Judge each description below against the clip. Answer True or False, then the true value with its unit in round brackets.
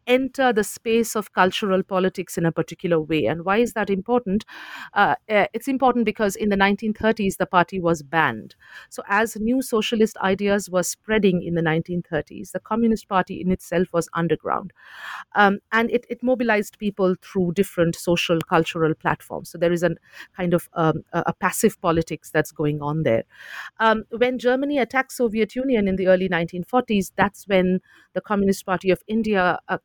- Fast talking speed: False (175 wpm)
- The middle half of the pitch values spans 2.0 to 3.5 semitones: False (4.2 semitones)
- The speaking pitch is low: False (190 Hz)